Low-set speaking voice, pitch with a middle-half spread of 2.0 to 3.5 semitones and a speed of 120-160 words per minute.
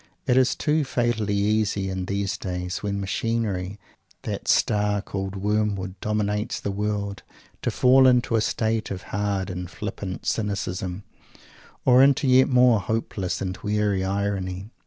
Yes: low, 105 Hz; narrow, 2.6 semitones; average, 145 wpm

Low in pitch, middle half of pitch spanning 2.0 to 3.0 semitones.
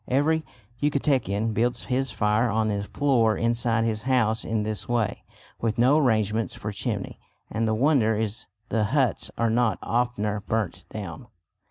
Yes: low, 115 Hz; narrow, 2.6 semitones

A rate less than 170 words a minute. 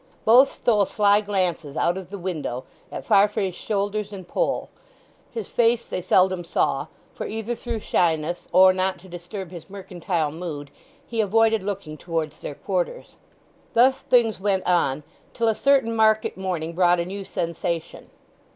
Yes: average, 155 wpm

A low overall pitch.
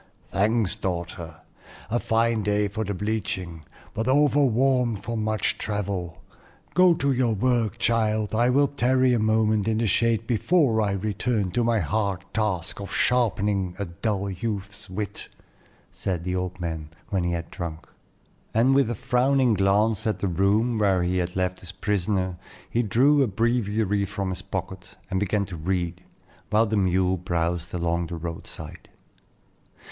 Yes: low, 105 Hz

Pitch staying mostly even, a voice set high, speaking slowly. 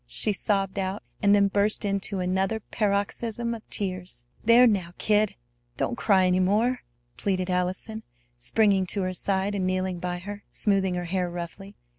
No: narrow, 2.1 semitones; high, 195 Hz; average, 160 wpm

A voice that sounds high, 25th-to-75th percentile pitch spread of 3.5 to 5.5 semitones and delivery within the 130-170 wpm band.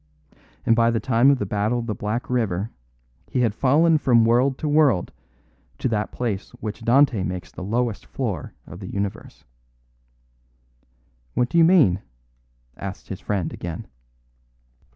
No: low, 115 Hz; average, 4.1 semitones; average, 150 wpm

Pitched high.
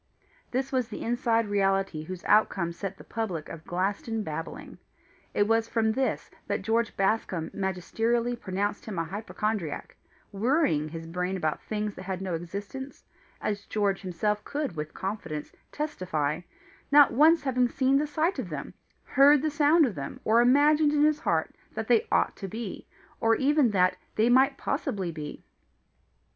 Yes: high, 215 Hz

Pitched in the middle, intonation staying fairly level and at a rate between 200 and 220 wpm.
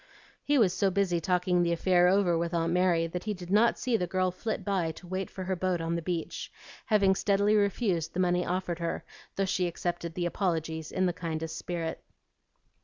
Yes: medium, 180 Hz; narrow, 2.1 semitones; fast, 205 wpm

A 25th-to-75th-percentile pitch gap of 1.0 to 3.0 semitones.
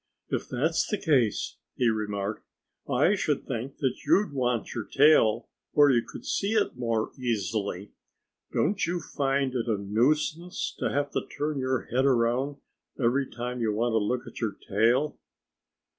No: average, 4.0 semitones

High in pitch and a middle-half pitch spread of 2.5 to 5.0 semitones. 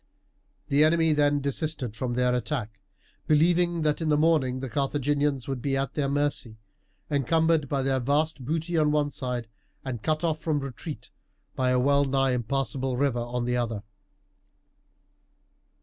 No: medium, 140 Hz; average, 3.3 semitones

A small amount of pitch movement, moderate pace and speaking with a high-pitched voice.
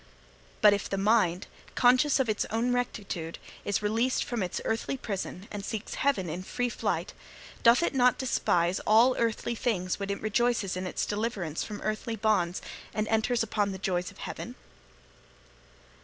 No: average, 3.7 semitones; average, 165 wpm; high, 215 Hz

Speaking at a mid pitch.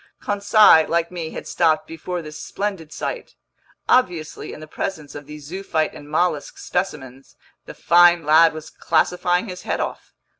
Yes: medium, 165 Hz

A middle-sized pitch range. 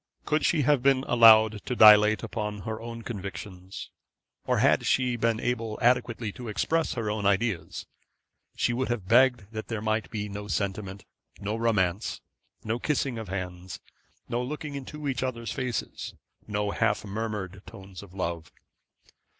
Yes: average, 3.2 semitones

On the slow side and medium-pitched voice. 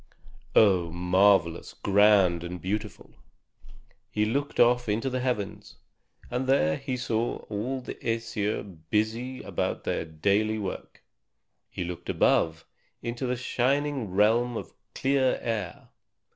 No: slow, 120 wpm; low, 110 Hz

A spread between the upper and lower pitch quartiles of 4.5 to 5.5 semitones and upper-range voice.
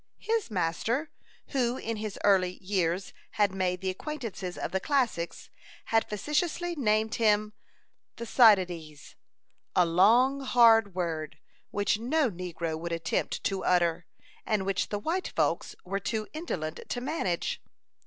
Yes: average, 5.0 semitones; high, 205 Hz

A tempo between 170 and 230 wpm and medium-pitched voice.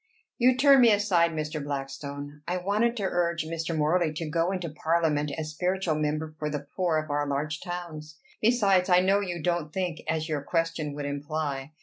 Yes: average, 190 wpm; medium, 160 Hz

